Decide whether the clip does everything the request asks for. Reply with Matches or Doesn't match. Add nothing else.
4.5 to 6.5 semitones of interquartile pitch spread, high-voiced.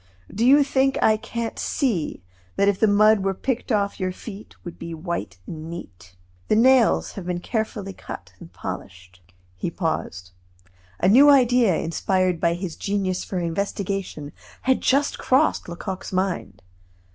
Matches